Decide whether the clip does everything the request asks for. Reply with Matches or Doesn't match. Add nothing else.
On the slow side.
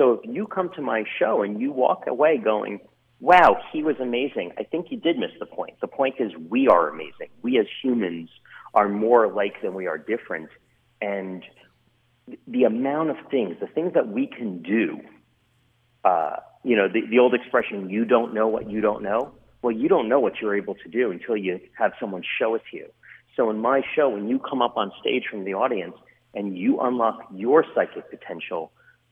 Doesn't match